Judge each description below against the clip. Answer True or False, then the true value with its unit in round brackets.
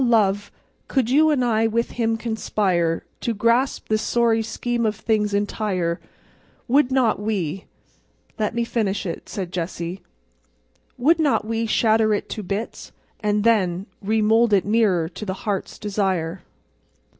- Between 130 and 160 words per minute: True (140 wpm)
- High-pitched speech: True (215 Hz)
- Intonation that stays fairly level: False (3.0 semitones)